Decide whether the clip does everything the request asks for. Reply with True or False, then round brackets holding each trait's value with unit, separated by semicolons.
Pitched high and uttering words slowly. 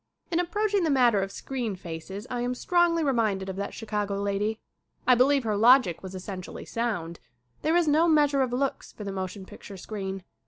False (225 Hz; 190 wpm)